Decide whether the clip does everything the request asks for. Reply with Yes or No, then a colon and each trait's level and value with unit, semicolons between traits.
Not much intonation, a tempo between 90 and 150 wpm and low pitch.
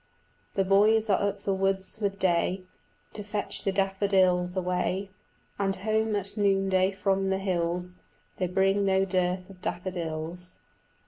No: narrow, 1.5 semitones; average, 140 wpm; high, 190 Hz